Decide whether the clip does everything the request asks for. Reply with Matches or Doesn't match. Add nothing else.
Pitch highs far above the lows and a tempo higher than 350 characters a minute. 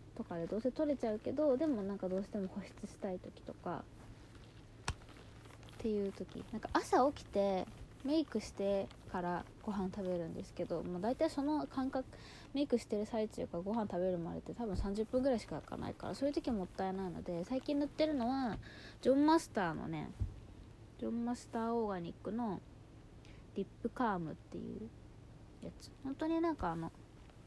Matches